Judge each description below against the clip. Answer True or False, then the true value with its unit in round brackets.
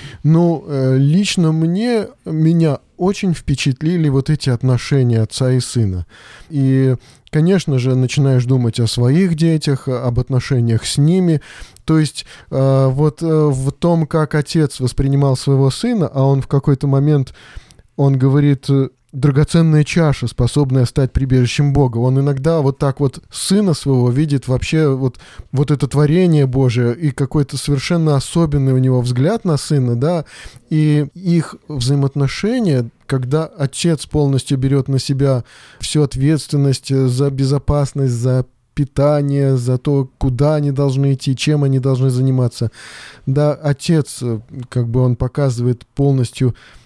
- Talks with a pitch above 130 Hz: True (140 Hz)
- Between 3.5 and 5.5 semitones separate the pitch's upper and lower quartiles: False (2.6 semitones)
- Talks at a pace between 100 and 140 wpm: True (135 wpm)